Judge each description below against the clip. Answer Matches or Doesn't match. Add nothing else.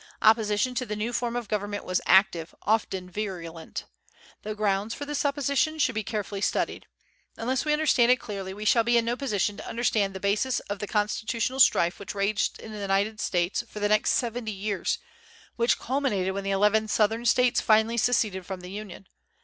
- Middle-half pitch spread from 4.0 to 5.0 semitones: Doesn't match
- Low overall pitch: Doesn't match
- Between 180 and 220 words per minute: Matches